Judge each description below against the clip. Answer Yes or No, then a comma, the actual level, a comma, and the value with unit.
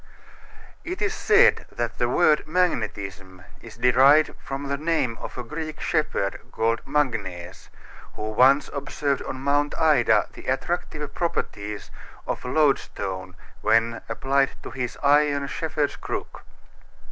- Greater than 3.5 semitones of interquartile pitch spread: Yes, average, 4.7 semitones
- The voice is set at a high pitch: No, low, 135 Hz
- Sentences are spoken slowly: Yes, slow, 125 wpm